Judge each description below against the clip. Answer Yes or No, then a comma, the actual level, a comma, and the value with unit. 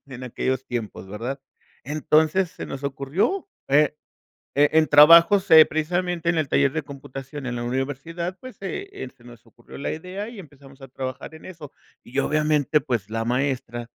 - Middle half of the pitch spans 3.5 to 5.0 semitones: Yes, average, 3.8 semitones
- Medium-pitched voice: Yes, medium, 145 Hz